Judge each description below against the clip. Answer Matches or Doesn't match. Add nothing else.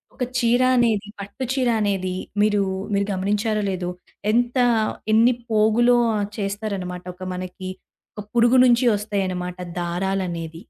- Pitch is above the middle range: Matches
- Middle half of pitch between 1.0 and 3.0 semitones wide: Doesn't match